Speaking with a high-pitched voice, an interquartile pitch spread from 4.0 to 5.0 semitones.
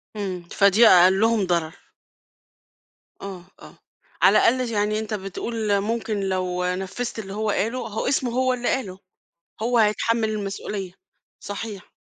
No: high, 210 Hz; average, 3.2 semitones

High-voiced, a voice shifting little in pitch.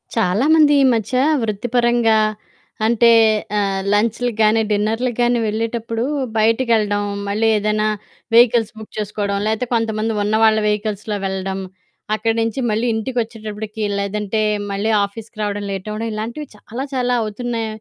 Yes: high, 220 Hz; narrow, 1.8 semitones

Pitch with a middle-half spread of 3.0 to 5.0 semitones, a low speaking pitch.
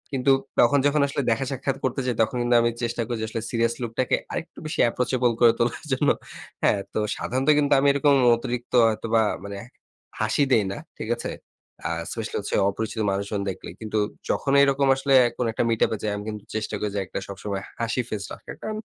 Yes: average, 3.6 semitones; low, 120 Hz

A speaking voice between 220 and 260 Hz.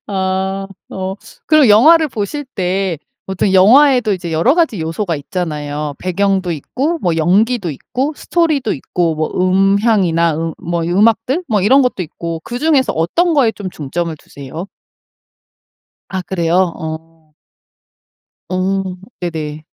No: high, 190 Hz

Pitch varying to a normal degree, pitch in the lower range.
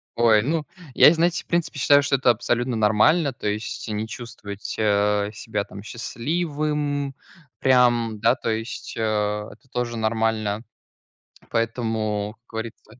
Yes: average, 3.9 semitones; low, 115 Hz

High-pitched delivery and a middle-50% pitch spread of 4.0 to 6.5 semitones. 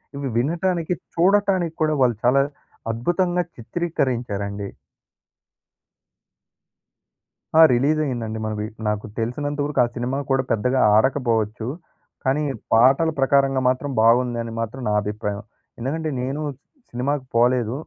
No: low, 130 Hz; average, 4.3 semitones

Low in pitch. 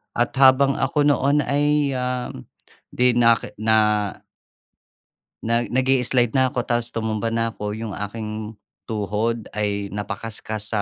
Yes: low, 115 Hz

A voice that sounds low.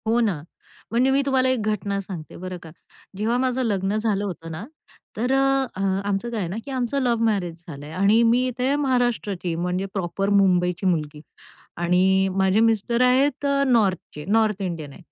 No: high, 205 Hz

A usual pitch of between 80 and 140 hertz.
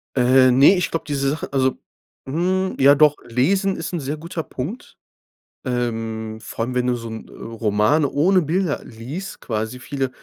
Yes: low, 135 Hz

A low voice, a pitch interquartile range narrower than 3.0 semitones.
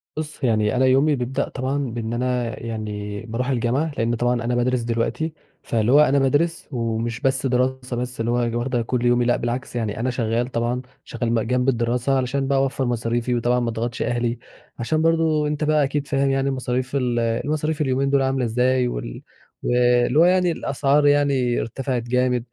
Yes: low, 125 Hz; narrow, 2.4 semitones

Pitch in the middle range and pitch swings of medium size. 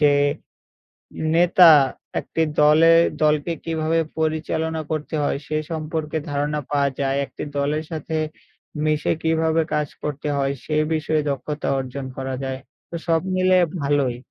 No: medium, 155 Hz; narrow, 2.0 semitones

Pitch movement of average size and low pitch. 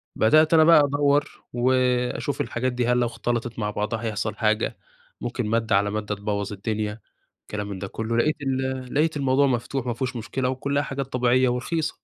Yes: average, 3.6 semitones; low, 125 Hz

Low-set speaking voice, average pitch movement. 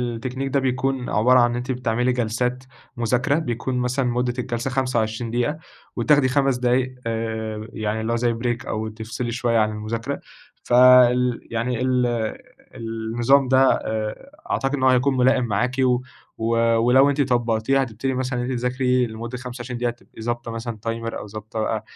No: low, 120 Hz; narrow, 2.0 semitones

